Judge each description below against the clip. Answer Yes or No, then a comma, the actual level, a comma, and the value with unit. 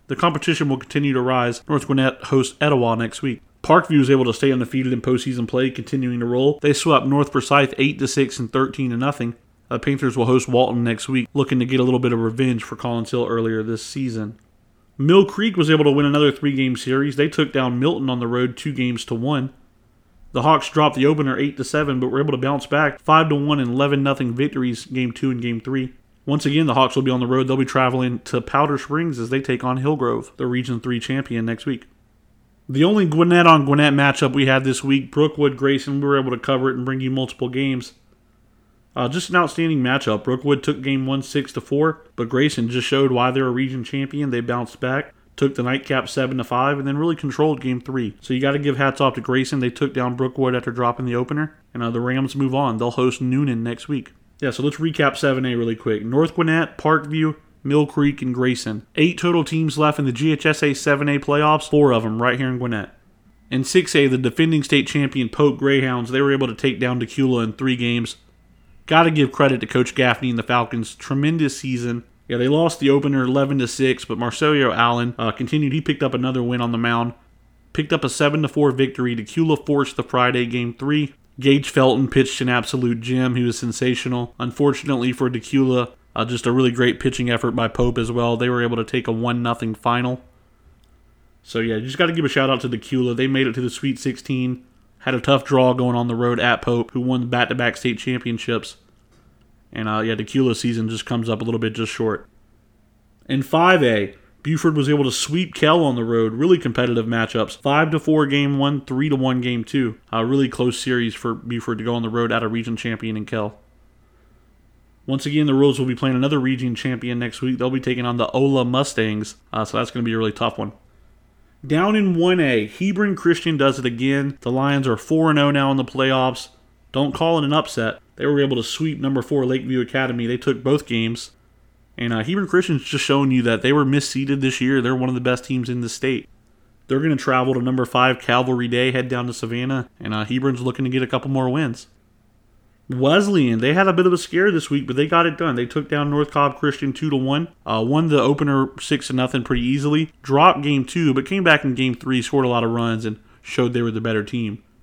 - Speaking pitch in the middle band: No, low, 130 Hz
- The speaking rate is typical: No, fast, 230 wpm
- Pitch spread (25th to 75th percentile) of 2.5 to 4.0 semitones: Yes, average, 2.9 semitones